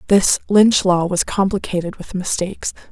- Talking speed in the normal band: Yes, average, 145 wpm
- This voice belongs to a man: No, female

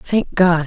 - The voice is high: No, medium, 175 Hz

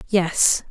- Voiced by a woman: Yes, female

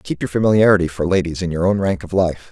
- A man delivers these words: Yes, male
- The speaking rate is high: Yes, fast, 265 wpm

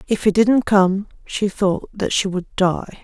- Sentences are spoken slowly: No, average, 200 wpm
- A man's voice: No, female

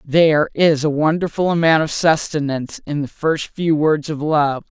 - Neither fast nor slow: Yes, average, 175 wpm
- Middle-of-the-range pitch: Yes, medium, 155 Hz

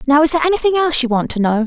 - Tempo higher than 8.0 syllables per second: Yes, 8.8 syllables/s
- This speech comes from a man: No, female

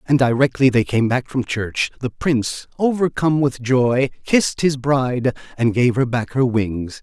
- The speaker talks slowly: No, average, 180 wpm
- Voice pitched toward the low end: Yes, low, 130 Hz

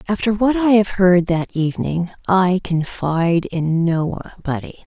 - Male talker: No, female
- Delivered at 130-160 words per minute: Yes, slow, 135 wpm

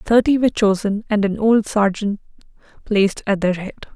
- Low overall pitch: No, high, 205 Hz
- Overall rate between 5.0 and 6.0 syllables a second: Yes, 5.3 syllables/s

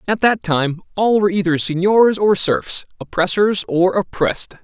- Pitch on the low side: No, high, 190 Hz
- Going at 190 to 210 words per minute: No, average, 155 wpm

